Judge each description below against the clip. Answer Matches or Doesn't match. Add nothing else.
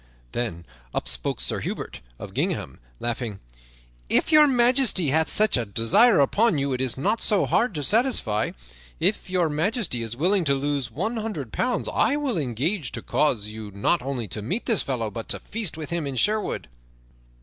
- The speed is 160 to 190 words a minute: Matches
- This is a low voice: Doesn't match